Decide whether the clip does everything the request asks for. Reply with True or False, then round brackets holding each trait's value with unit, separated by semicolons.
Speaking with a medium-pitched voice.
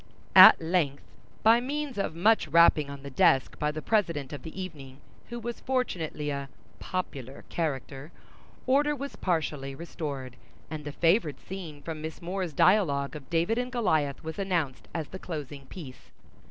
True (160 Hz)